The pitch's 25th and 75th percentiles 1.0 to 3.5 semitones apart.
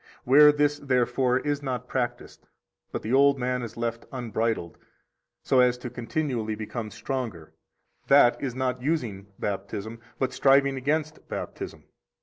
Yes: average, 3.1 semitones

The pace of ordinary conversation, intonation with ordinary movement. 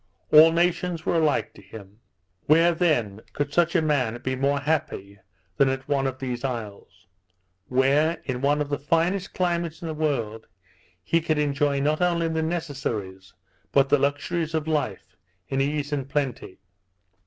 Yes: average, 165 wpm; average, 3.4 semitones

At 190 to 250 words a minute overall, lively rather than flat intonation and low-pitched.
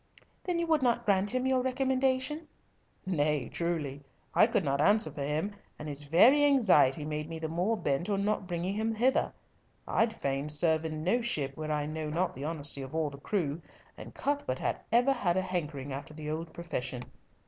No: average, 195 wpm; wide, 7.2 semitones; medium, 170 Hz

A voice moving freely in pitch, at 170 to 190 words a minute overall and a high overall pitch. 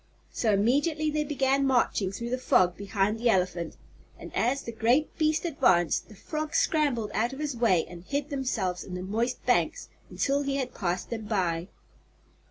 Yes: wide, 6.4 semitones; average, 175 wpm; high, 235 Hz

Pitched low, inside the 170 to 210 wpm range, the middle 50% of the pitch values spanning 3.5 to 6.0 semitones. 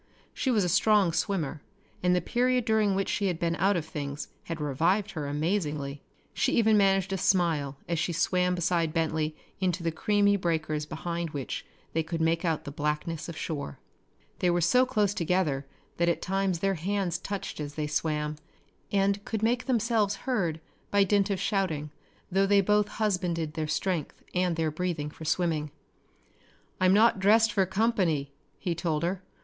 No: medium, 175 Hz; average, 175 wpm; average, 4.0 semitones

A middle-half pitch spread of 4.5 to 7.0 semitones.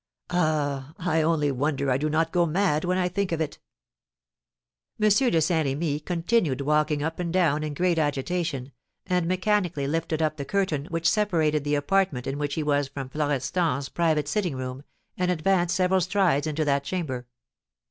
No: average, 3.7 semitones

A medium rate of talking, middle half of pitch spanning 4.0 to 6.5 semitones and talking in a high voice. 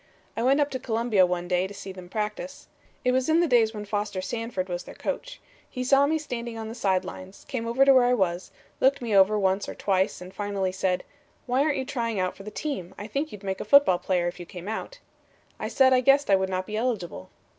No: fast, 245 wpm; average, 5.3 semitones; high, 215 Hz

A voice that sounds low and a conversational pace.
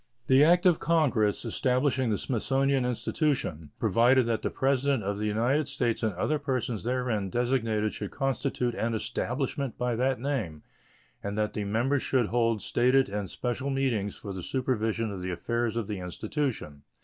Yes: low, 120 Hz; average, 165 wpm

